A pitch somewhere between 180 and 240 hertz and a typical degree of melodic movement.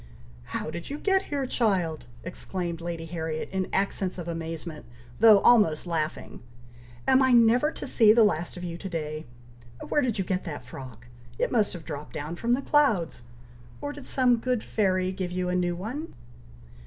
No: medium, 185 Hz; wide, 6.2 semitones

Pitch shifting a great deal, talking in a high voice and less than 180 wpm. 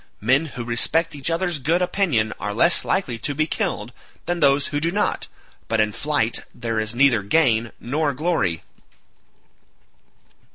No: wide, 6.2 semitones; medium, 140 Hz; average, 155 wpm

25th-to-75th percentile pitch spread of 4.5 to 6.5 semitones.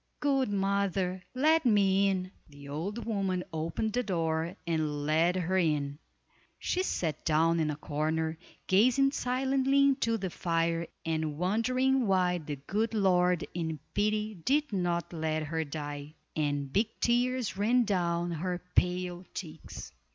Yes: average, 5.2 semitones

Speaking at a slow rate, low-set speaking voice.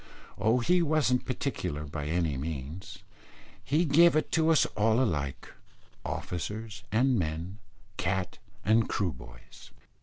Yes: slow, 125 wpm; low, 100 Hz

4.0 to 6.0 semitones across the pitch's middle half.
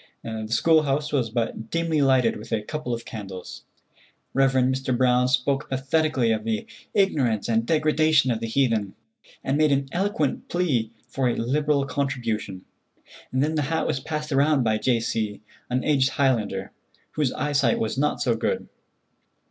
Yes: average, 4.5 semitones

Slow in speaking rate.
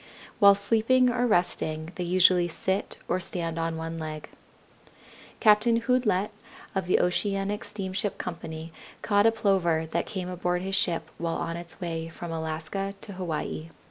No: average, 150 wpm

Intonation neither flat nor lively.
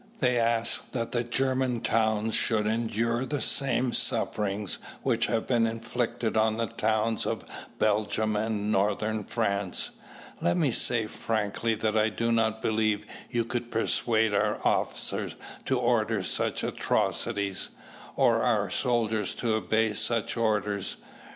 No: narrow, 1.6 semitones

